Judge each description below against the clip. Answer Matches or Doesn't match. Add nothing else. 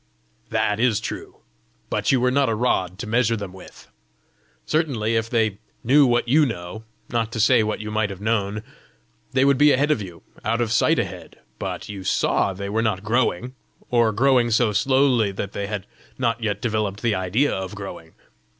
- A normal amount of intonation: Matches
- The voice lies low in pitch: Matches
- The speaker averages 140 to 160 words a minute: Doesn't match